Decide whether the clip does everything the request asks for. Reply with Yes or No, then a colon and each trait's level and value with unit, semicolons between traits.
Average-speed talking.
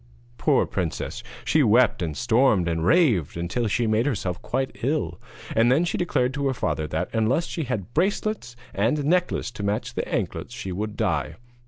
Yes: average, 180 wpm